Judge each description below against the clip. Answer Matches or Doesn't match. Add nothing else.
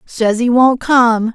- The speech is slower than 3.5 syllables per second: Matches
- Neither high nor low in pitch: Doesn't match